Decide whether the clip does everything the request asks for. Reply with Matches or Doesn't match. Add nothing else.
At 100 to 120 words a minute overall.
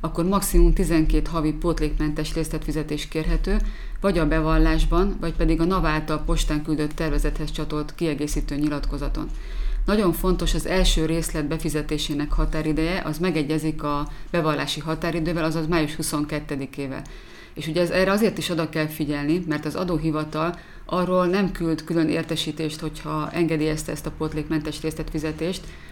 Doesn't match